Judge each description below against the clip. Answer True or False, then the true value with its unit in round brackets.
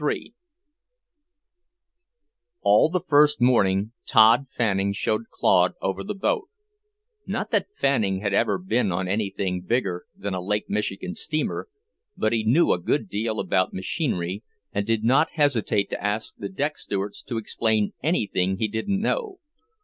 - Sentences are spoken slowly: False (150 wpm)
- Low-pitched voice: True (110 Hz)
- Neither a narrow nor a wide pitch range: False (5.7 semitones)